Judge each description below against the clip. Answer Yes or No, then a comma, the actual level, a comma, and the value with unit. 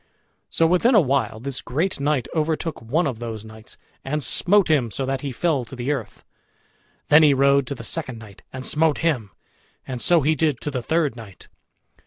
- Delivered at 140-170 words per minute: No, average, 200 wpm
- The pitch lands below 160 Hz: Yes, medium, 140 Hz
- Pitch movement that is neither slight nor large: Yes, average, 4.6 semitones